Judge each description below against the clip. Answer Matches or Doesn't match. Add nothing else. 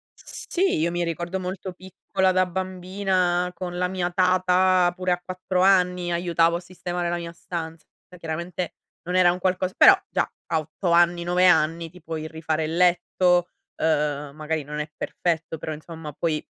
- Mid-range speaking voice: Matches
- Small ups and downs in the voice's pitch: Matches